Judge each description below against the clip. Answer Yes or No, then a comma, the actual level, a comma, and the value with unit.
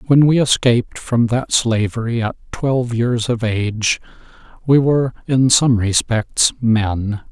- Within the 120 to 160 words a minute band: Yes, average, 140 wpm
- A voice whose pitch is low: Yes, low, 120 Hz